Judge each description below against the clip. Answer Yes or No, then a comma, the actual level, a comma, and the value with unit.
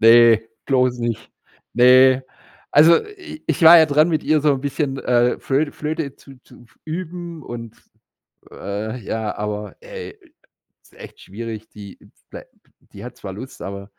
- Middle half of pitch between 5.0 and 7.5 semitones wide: Yes, wide, 5.6 semitones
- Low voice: Yes, low, 130 Hz